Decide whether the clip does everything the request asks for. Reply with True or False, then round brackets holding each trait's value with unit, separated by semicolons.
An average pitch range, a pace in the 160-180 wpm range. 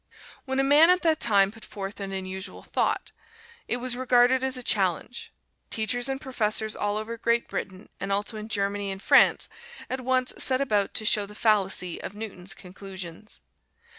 True (4.2 semitones; 175 wpm)